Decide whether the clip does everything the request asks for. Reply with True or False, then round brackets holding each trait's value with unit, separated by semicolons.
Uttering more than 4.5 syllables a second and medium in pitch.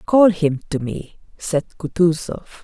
False (4.2 syllables/s; 165 Hz)